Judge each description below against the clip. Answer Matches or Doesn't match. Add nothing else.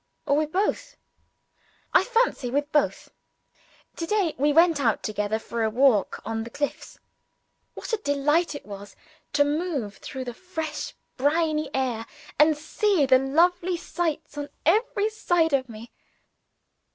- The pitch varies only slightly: Doesn't match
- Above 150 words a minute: Doesn't match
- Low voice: Doesn't match